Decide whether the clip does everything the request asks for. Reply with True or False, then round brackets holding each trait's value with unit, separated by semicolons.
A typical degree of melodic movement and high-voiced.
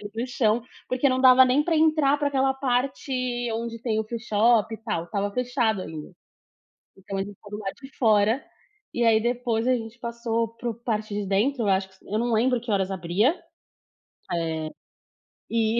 True (3.4 semitones; 230 Hz)